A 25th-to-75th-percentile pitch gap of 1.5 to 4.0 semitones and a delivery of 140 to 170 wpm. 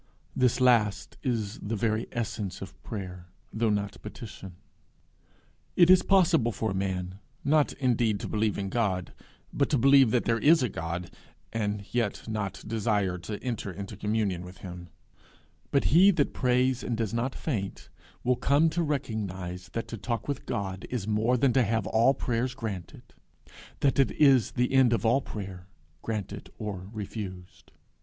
No: average, 4.4 semitones; average, 165 wpm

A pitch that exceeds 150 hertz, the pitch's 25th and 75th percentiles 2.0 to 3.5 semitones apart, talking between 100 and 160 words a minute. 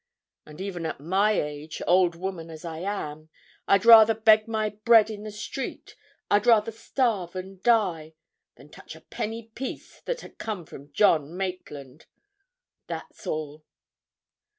No: high, 190 Hz; average, 5.2 semitones; average, 150 wpm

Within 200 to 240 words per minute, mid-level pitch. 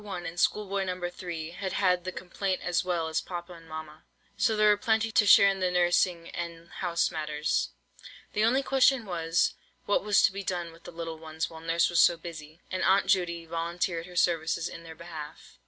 Yes: fast, 205 wpm; medium, 175 Hz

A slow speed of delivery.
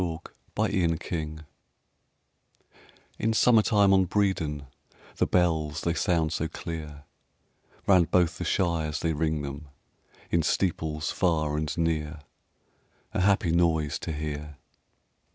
Yes: slow, 120 wpm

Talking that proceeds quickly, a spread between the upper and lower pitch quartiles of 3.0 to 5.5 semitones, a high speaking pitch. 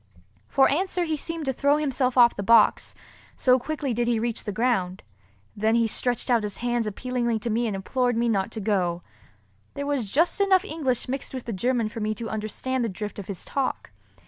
Yes: fast, 215 wpm; average, 3.7 semitones; high, 240 Hz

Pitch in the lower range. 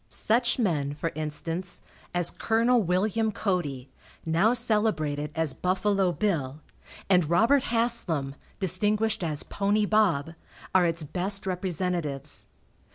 No: medium, 185 Hz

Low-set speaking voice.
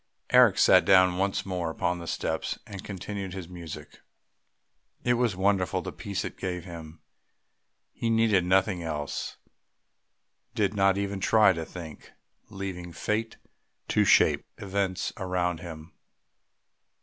Yes: very low, 95 Hz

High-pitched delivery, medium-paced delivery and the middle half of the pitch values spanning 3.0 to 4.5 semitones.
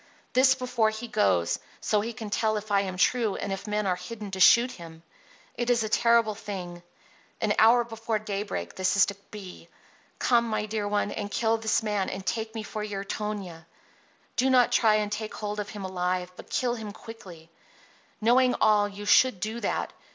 No: high, 210 Hz; average, 195 wpm; narrow, 2.5 semitones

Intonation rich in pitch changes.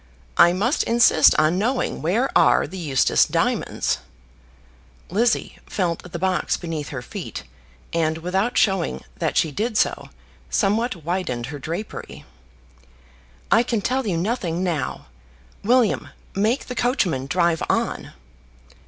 Yes: wide, 5.7 semitones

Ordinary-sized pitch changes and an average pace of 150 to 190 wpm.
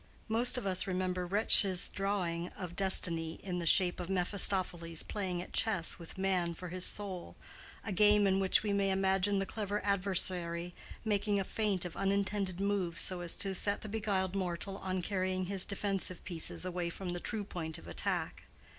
No: narrow, 2.1 semitones; average, 180 wpm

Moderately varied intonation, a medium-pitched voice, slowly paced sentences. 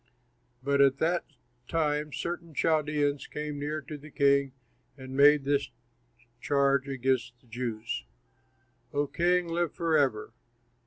No: narrow, 2.2 semitones; medium, 145 Hz; slow, 120 wpm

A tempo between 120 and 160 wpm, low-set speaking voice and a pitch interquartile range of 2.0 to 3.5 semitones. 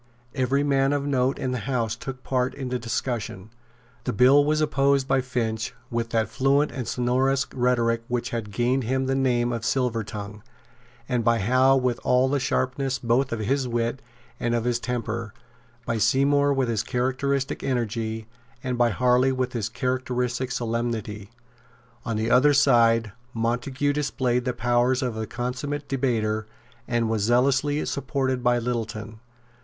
Yes: average, 155 wpm; low, 125 Hz; narrow, 2.4 semitones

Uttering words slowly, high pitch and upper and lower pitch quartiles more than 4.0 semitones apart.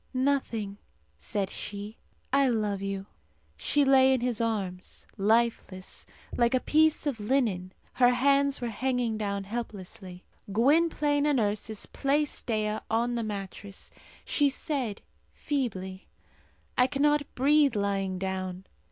Yes: slow, 125 wpm; high, 230 Hz; wide, 5.4 semitones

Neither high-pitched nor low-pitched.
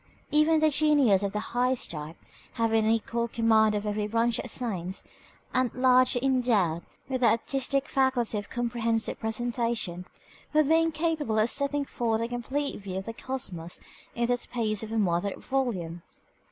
No: high, 235 Hz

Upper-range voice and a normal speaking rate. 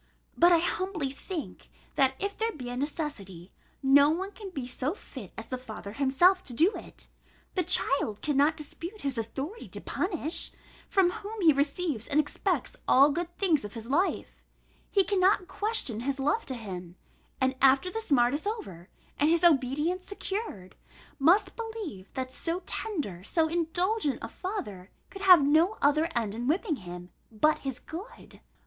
Yes: very high, 300 Hz; average, 170 wpm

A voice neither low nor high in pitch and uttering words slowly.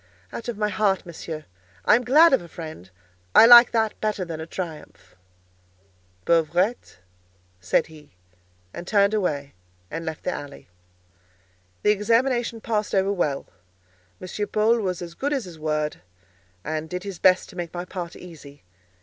No: medium, 180 Hz; average, 160 wpm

